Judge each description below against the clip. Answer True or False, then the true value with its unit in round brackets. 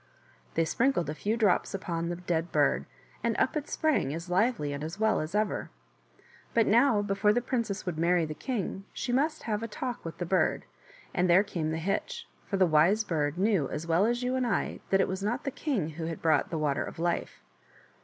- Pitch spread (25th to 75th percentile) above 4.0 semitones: True (5.5 semitones)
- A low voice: False (190 Hz)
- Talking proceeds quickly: True (220 wpm)